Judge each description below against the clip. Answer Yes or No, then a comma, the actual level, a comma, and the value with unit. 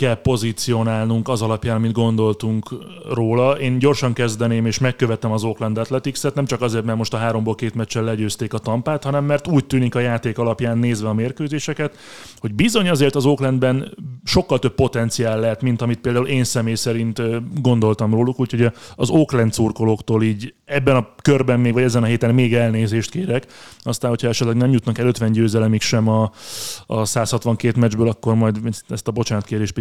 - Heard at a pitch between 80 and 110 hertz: No, low, 120 Hz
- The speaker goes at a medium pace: No, fast, 175 wpm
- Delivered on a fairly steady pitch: Yes, narrow, 2.3 semitones